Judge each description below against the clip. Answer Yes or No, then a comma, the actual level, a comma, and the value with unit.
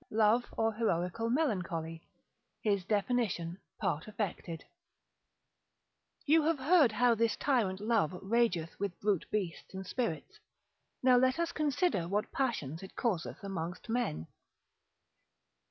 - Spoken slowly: Yes, slow, 120 wpm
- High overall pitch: Yes, high, 210 Hz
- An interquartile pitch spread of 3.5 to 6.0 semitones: Yes, average, 5.3 semitones